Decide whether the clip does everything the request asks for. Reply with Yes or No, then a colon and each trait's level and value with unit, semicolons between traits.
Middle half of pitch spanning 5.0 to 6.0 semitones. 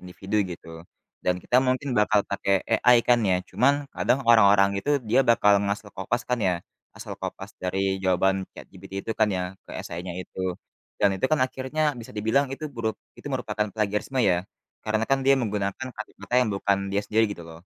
No: average, 3.8 semitones